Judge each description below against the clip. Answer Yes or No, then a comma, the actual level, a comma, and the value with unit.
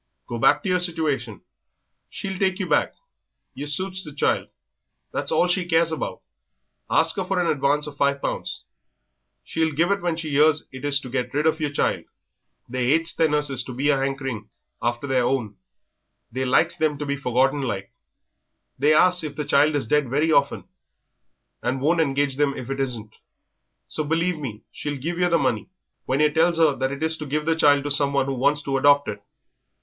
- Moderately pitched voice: Yes, medium, 145 Hz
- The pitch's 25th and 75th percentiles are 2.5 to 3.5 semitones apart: Yes, average, 3.1 semitones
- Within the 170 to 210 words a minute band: Yes, average, 200 wpm